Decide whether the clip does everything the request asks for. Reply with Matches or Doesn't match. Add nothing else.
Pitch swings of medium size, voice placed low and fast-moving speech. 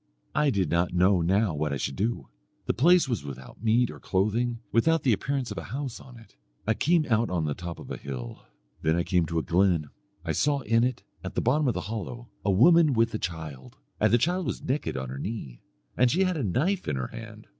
Doesn't match